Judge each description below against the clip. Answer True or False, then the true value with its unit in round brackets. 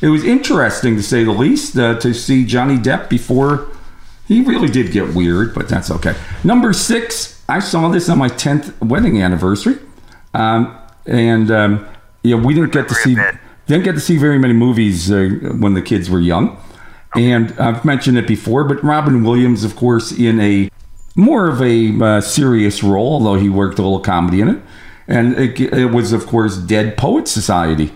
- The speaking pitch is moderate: False (115 Hz)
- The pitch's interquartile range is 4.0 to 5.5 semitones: True (4.6 semitones)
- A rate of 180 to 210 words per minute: True (190 wpm)